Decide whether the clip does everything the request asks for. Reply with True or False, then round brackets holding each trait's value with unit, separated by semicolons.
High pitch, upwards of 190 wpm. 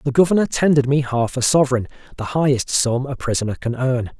False (135 Hz; 200 wpm)